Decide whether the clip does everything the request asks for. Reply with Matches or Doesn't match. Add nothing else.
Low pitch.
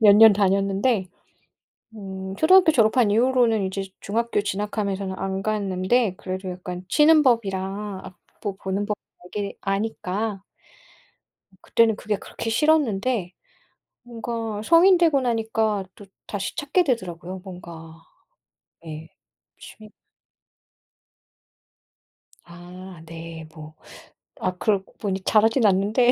Doesn't match